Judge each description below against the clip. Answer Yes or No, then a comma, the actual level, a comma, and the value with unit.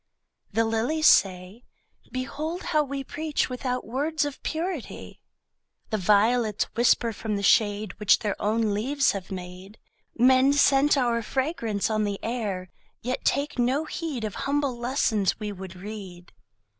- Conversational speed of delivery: Yes, average, 145 wpm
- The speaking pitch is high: Yes, high, 235 Hz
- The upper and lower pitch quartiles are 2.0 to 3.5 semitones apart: No, average, 5.1 semitones